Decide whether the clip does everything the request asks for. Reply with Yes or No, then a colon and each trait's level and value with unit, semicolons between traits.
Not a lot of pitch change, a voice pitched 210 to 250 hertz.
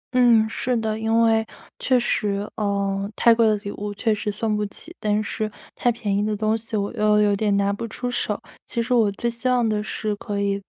Yes: narrow, 2.1 semitones; high, 215 Hz